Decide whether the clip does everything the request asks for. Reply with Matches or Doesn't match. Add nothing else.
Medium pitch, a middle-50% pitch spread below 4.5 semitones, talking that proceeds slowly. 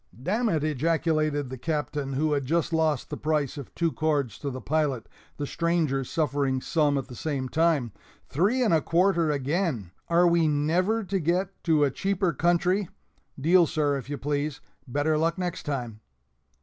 Doesn't match